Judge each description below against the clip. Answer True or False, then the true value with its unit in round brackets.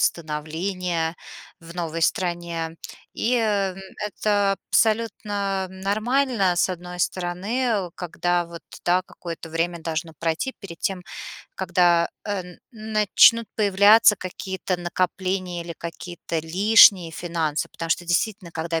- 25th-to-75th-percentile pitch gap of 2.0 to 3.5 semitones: True (3.1 semitones)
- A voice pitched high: False (180 Hz)